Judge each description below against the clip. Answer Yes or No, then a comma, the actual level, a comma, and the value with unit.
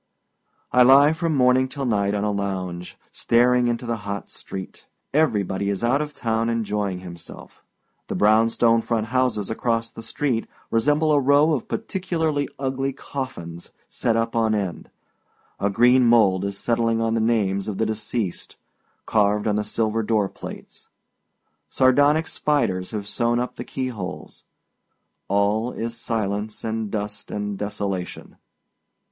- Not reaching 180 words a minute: Yes, average, 150 wpm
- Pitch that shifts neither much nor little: Yes, average, 3.7 semitones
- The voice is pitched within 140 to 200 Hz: No, low, 115 Hz